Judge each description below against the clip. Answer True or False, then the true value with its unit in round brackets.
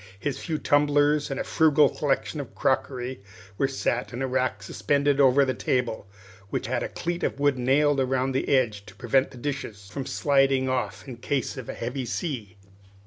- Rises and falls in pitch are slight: True (2.3 semitones)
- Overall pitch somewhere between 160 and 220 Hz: False (135 Hz)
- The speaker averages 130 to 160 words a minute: False (190 wpm)